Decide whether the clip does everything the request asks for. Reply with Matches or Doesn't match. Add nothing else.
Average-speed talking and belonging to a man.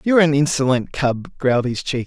Doesn't match